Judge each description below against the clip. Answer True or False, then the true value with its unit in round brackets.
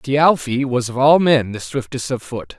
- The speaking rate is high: True (210 wpm)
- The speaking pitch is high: False (135 Hz)